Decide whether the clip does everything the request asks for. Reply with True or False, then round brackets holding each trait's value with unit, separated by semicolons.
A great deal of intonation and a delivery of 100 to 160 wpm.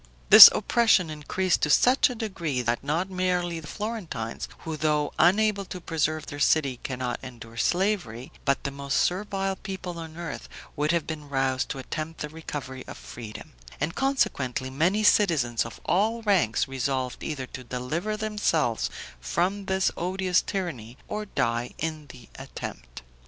True (6.3 semitones; 155 wpm)